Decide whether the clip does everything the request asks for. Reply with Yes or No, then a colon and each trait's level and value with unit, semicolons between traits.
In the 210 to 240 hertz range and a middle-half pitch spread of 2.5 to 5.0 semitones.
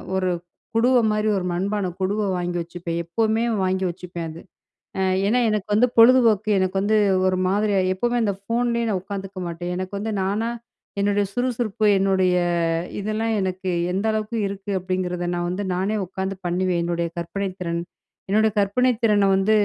No: high, 195 Hz; average, 2.8 semitones